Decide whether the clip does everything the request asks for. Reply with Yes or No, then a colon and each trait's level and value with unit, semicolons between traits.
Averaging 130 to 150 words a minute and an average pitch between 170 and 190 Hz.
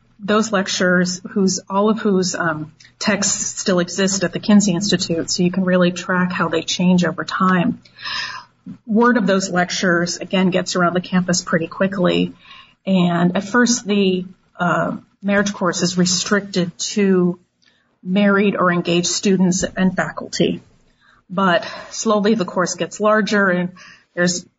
Yes: average, 145 wpm; medium, 185 Hz